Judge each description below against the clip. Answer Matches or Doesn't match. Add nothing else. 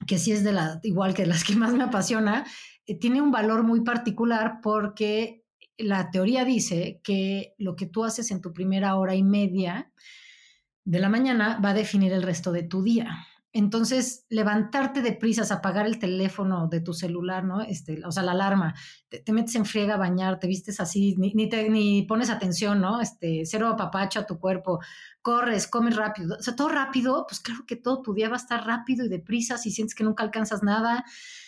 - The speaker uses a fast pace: Matches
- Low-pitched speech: Doesn't match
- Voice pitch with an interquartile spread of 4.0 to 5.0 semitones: Doesn't match